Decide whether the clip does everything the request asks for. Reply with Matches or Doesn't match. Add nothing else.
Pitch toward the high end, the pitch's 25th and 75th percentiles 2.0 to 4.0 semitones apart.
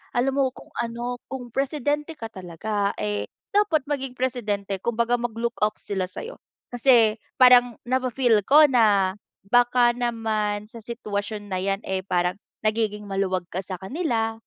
Matches